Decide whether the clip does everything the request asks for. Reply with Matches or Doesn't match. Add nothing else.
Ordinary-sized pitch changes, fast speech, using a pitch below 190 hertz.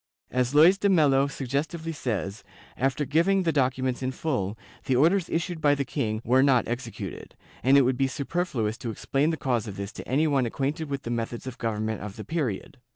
Matches